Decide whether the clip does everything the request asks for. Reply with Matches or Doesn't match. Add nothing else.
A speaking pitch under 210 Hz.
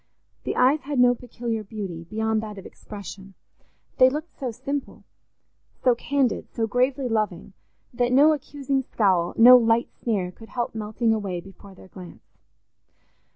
Doesn't match